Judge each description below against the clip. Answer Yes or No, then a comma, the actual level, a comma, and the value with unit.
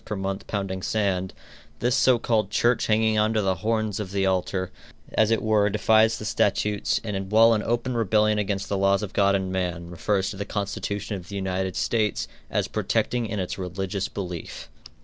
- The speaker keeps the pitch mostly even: Yes, narrow, 2.3 semitones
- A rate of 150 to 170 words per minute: No, average, 195 wpm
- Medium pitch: No, low, 100 Hz